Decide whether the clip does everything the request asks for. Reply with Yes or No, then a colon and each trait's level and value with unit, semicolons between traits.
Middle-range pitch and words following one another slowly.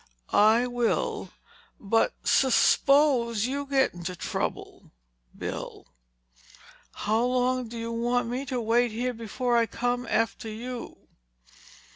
No: high, 240 Hz; slow, 120 wpm